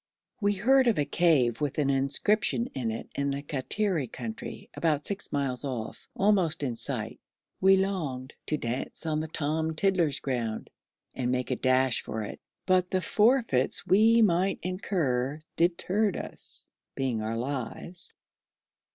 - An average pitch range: No, wide, 6.6 semitones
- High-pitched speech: No, medium, 150 Hz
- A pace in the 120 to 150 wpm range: Yes, average, 145 wpm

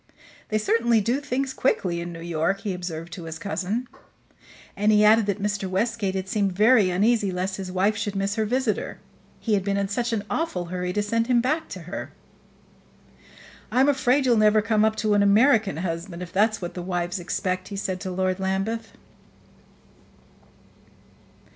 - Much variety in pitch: No, average, 3.4 semitones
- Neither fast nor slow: Yes, average, 180 wpm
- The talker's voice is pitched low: No, high, 200 Hz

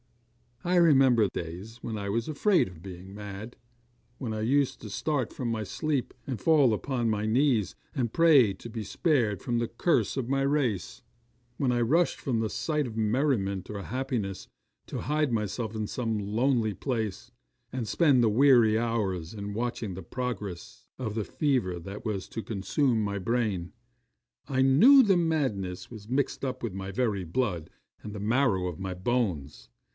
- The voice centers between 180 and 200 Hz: No, low, 115 Hz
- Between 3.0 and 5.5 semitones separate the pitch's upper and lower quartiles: Yes, average, 4.7 semitones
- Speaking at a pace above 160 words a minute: Yes, average, 170 wpm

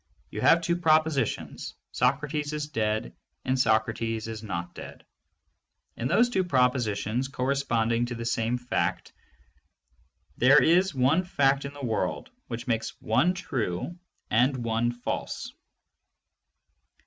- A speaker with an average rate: No, slow, 125 wpm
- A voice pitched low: Yes, low, 125 Hz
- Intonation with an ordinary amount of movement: Yes, average, 4.5 semitones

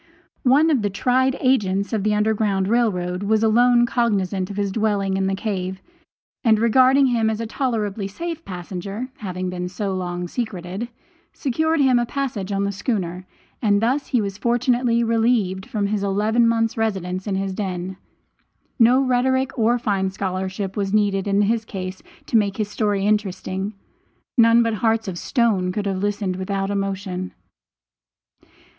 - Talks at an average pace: Yes, average, 165 wpm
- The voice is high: Yes, high, 210 Hz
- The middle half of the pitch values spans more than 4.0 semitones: No, average, 3.4 semitones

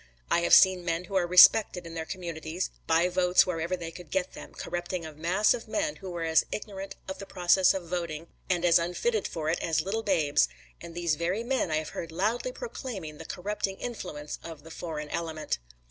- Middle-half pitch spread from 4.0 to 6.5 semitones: No, average, 2.8 semitones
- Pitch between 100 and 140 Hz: No, medium, 175 Hz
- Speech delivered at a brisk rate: Yes, fast, 210 wpm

